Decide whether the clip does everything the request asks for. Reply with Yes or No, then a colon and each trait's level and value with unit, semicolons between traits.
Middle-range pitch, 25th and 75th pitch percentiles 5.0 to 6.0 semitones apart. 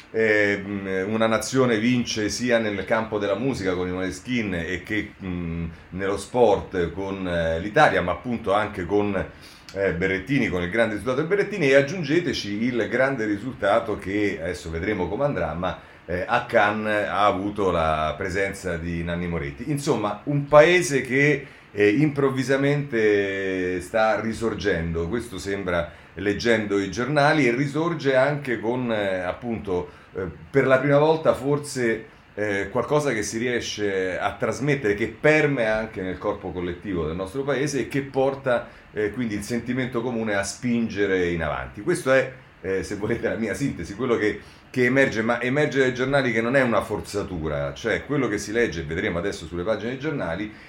No: low, 105 Hz; wide, 5.5 semitones